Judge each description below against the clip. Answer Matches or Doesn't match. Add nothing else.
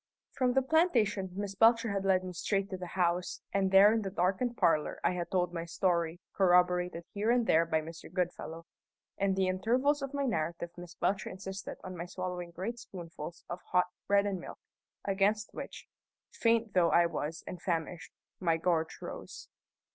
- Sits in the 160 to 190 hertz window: Matches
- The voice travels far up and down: Doesn't match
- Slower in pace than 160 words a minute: Doesn't match